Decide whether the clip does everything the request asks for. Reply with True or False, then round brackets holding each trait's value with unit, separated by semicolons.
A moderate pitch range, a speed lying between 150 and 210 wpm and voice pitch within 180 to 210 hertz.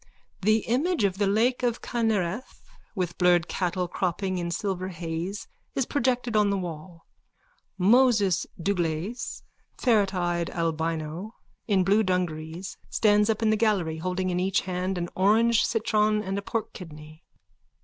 False (3.8 semitones; 140 wpm; 190 Hz)